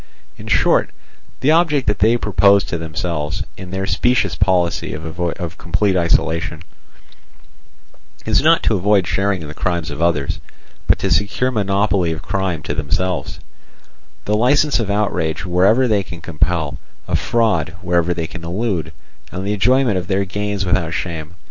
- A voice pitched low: Yes, very low, 90 Hz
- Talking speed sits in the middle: Yes, average, 155 wpm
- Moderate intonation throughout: Yes, average, 3.6 semitones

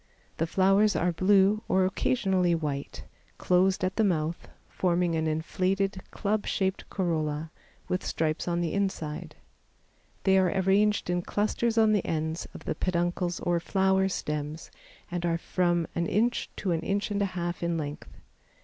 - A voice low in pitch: No, medium, 180 Hz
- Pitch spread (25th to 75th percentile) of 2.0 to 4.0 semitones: Yes, average, 2.7 semitones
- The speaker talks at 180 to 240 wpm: No, average, 160 wpm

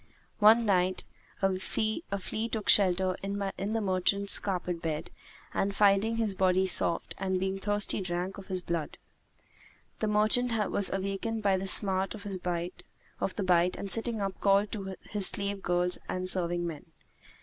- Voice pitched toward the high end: Yes, high, 195 Hz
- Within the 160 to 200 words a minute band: No, average, 150 wpm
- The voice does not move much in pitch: Yes, narrow, 2.1 semitones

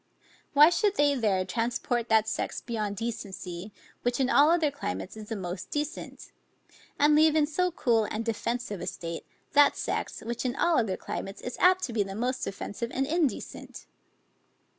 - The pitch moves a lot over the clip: Yes, wide, 5.8 semitones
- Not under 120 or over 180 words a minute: Yes, average, 175 wpm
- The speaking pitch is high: Yes, high, 240 Hz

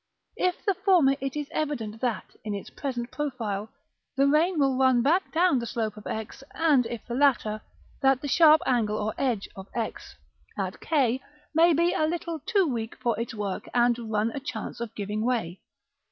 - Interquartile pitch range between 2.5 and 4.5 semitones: No, wide, 5.4 semitones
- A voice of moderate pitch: No, very high, 250 Hz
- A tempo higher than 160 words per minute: Yes, average, 190 wpm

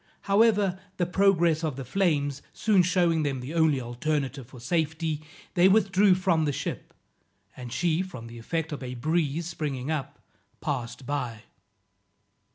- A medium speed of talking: Yes, average, 150 wpm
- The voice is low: No, medium, 155 Hz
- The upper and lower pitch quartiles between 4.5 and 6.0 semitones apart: Yes, average, 4.8 semitones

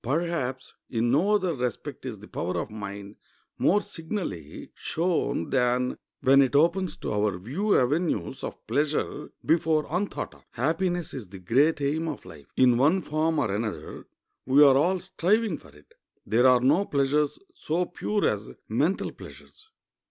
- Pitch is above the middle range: No, medium, 145 Hz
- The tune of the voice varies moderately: No, wide, 5.8 semitones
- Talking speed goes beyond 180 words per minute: No, average, 160 wpm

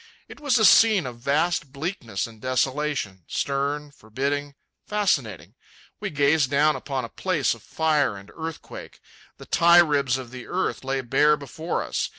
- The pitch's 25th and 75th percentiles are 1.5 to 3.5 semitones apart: No, average, 3.9 semitones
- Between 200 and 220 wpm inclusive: No, average, 155 wpm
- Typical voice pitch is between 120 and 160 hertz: Yes, medium, 140 Hz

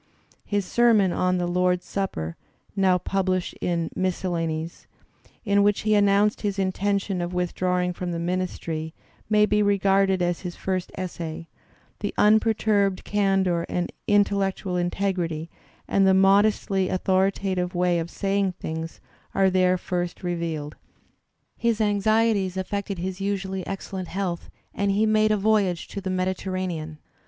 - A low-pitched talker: No, high, 190 Hz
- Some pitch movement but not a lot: No, narrow, 2.1 semitones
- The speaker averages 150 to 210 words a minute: No, average, 140 wpm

